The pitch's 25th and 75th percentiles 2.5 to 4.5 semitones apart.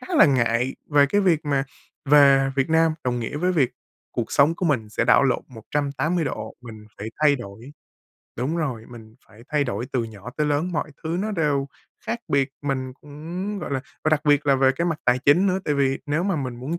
Yes: average, 4.0 semitones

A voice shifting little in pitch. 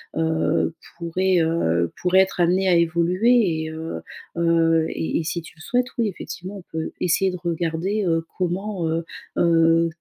Yes: narrow, 2.3 semitones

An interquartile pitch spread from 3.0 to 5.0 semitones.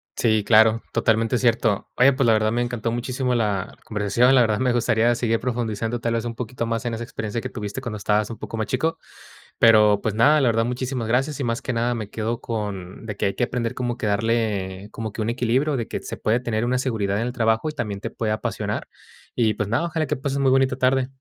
No: narrow, 2.4 semitones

